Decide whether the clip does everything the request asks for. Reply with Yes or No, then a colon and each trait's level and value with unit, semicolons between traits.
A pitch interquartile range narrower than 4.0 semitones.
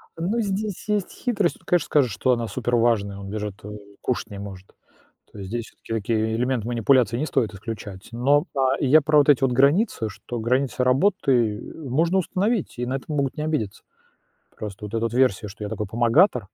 No: average, 5.3 semitones